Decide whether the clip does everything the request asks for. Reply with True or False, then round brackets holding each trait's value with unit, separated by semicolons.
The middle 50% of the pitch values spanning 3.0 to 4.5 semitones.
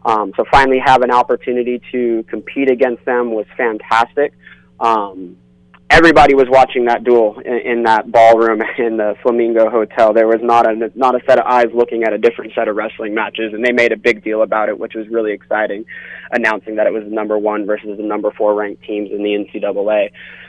False (2.4 semitones)